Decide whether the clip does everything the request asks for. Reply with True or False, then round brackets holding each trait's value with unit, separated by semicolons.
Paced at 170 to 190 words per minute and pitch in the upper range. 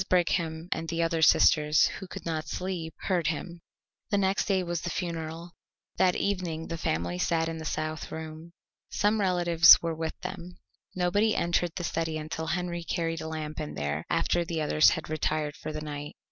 False (185 wpm; 165 Hz)